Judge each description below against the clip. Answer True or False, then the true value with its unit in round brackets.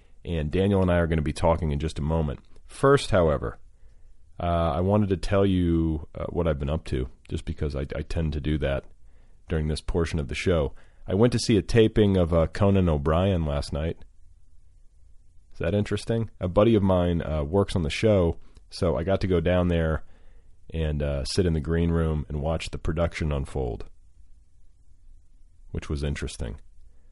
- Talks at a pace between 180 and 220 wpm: True (195 wpm)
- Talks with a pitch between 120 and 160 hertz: False (85 Hz)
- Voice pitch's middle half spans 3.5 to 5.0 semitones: False (2.8 semitones)